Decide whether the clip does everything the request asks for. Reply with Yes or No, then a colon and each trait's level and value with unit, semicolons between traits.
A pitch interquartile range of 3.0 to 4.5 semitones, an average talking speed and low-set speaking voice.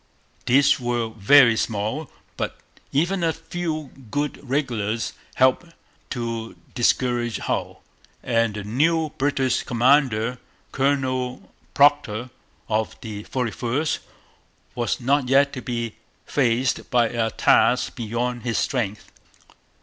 No: average, 3.4 semitones; slow, 110 wpm; low, 125 Hz